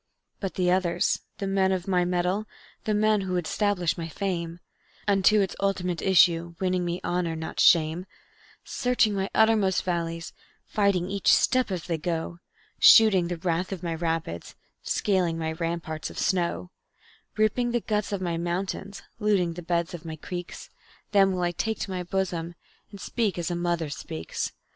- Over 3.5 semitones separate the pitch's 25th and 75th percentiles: No, narrow, 2.6 semitones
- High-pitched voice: No, medium, 180 Hz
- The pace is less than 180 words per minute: Yes, average, 170 wpm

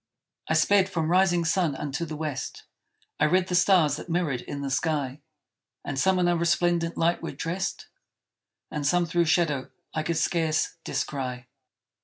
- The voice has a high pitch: No, medium, 165 Hz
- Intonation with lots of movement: No, average, 3.0 semitones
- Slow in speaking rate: No, average, 165 wpm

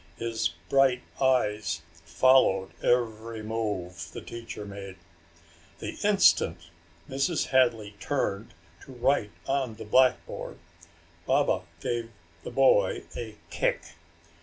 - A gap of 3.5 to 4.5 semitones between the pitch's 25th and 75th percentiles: Yes, average, 4.2 semitones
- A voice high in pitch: No, low, 115 Hz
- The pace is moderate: No, slow, 105 wpm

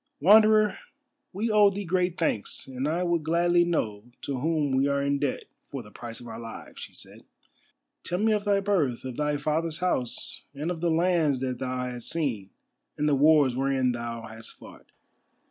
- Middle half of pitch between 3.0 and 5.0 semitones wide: No, wide, 5.5 semitones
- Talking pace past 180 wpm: Yes, average, 190 wpm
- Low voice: No, medium, 150 Hz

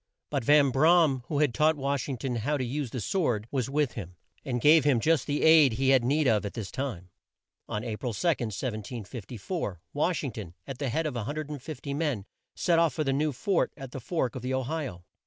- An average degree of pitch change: Yes, average, 4.2 semitones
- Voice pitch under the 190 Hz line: Yes, low, 135 Hz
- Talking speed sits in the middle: No, fast, 230 wpm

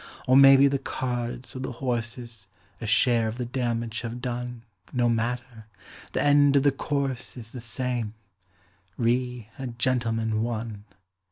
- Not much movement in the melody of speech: Yes, narrow, 2.0 semitones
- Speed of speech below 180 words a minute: Yes, average, 150 wpm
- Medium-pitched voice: No, low, 120 Hz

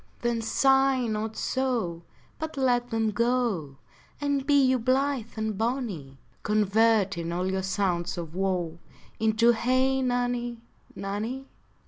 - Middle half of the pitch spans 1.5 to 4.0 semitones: No, average, 4.8 semitones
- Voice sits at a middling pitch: No, high, 230 Hz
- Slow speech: Yes, slow, 120 wpm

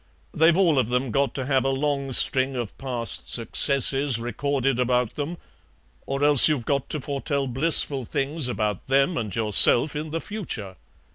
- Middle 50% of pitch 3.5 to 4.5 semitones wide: No, average, 2.8 semitones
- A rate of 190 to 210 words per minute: No, average, 165 wpm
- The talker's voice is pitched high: No, low, 135 Hz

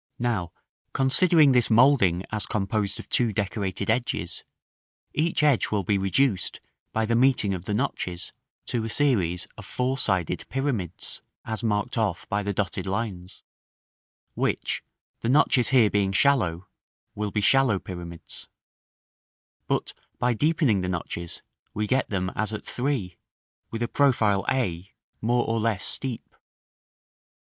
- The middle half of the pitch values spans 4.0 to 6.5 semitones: Yes, average, 4.7 semitones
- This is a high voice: No, low, 110 Hz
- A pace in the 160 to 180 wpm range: No, average, 140 wpm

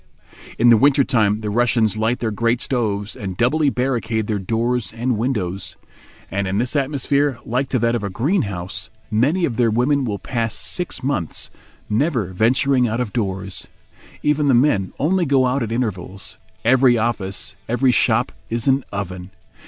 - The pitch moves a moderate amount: Yes, average, 4.2 semitones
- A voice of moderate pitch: No, low, 115 Hz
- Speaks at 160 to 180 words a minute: Yes, average, 170 wpm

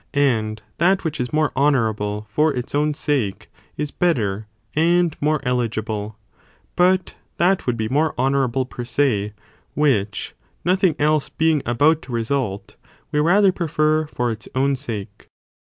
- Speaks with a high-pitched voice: No, medium, 140 Hz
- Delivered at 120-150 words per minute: Yes, average, 145 wpm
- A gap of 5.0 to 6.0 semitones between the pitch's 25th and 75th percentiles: Yes, wide, 5.5 semitones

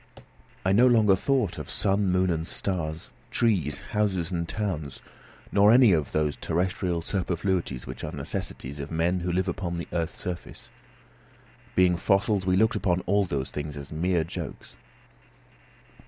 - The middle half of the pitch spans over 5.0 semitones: No, average, 3.2 semitones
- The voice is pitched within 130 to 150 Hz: No, very low, 90 Hz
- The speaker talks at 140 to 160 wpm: Yes, average, 155 wpm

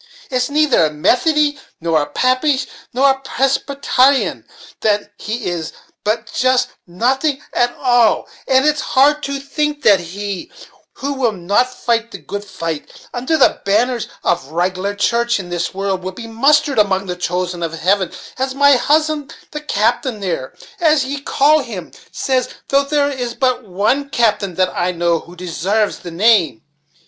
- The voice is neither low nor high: No, high, 235 Hz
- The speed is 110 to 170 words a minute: Yes, average, 160 wpm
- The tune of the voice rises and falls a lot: Yes, wide, 6.6 semitones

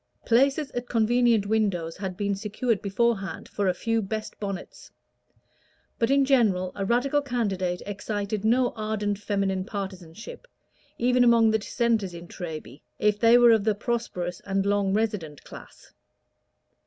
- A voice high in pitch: Yes, high, 210 Hz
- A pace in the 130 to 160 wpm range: Yes, average, 140 wpm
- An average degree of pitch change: Yes, average, 3.4 semitones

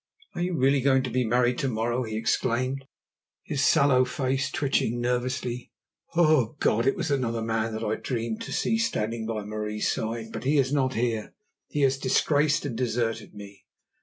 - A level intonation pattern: No, average, 3.1 semitones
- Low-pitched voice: Yes, low, 125 Hz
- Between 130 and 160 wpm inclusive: No, average, 180 wpm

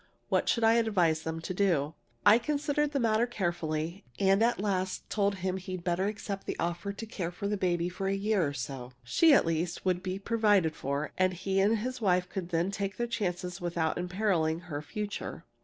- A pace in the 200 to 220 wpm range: Yes, fast, 205 wpm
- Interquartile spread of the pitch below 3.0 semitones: No, average, 3.4 semitones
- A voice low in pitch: No, high, 190 Hz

